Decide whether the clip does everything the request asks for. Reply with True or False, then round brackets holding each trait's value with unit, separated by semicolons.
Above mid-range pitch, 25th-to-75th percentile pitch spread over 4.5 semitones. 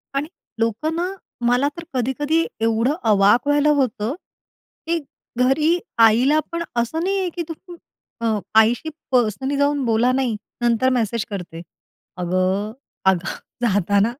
True (245 Hz; 5.5 semitones)